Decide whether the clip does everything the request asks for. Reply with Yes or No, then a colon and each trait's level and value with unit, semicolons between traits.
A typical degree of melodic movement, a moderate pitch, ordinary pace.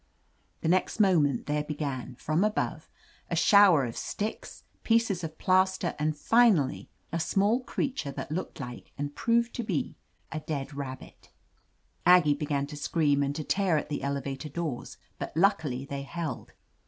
Yes: average, 5.0 semitones; medium, 155 Hz; average, 155 wpm